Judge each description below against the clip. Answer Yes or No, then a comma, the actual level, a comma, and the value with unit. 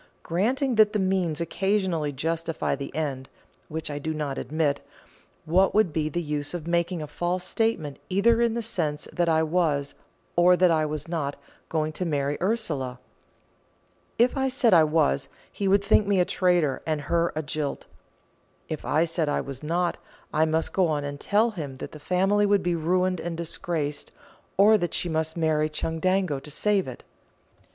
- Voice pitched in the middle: Yes, medium, 165 Hz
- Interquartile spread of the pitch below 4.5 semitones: Yes, average, 3.7 semitones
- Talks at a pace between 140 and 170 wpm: No, average, 180 wpm